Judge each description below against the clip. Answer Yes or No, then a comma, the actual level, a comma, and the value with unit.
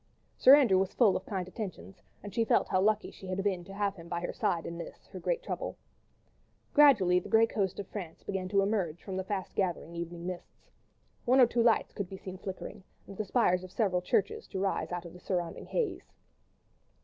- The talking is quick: Yes, fast, 220 wpm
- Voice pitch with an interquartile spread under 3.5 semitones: Yes, average, 2.8 semitones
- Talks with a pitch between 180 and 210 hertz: Yes, high, 190 Hz